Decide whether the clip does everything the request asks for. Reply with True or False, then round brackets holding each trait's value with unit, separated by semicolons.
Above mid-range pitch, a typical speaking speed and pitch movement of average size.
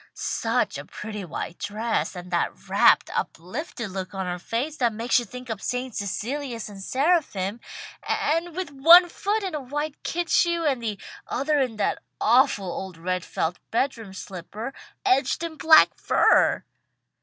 False (240 Hz; 160 wpm; 7.1 semitones)